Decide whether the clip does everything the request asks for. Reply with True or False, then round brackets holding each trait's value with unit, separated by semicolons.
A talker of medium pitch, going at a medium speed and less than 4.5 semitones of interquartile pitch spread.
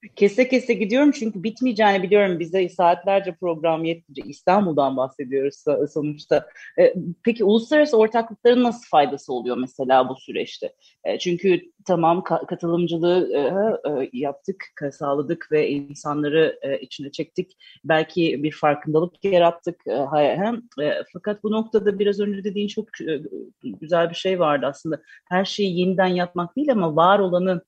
False (175 Hz; 120 wpm; 5.1 semitones)